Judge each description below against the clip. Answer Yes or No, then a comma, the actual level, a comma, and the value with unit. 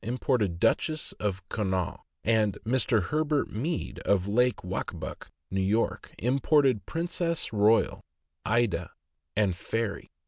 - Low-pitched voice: Yes, low, 110 Hz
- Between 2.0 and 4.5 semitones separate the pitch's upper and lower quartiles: No, average, 5.0 semitones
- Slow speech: Yes, slow, 105 wpm